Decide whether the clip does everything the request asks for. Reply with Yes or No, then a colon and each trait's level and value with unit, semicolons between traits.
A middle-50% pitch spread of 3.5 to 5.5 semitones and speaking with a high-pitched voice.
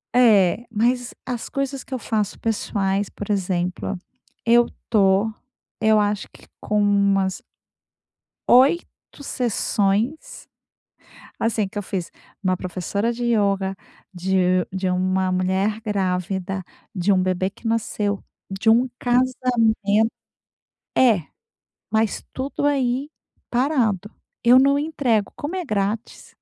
Yes: average, 4.0 semitones; high, 210 Hz